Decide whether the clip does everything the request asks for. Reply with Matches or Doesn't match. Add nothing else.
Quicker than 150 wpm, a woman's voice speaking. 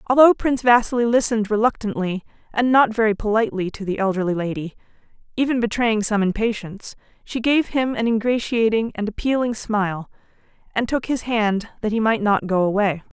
Matches